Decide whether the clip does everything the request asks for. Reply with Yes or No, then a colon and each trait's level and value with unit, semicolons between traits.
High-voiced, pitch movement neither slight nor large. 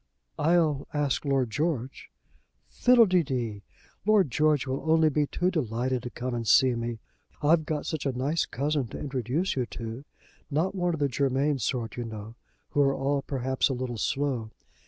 No: low, 135 Hz; average, 3.8 semitones